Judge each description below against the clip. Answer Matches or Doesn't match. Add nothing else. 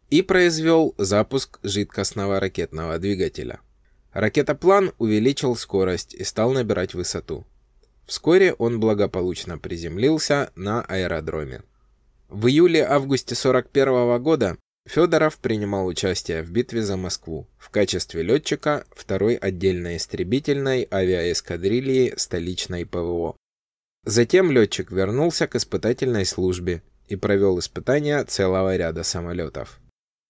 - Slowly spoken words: Matches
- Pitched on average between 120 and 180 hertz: Doesn't match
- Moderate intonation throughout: Doesn't match